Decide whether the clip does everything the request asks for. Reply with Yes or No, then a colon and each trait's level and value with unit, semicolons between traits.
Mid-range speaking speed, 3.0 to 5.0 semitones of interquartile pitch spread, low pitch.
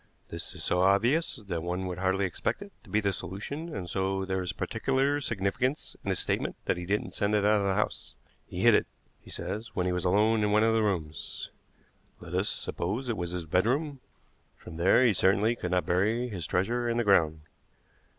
No: fast, 215 wpm; average, 4.0 semitones; low, 100 Hz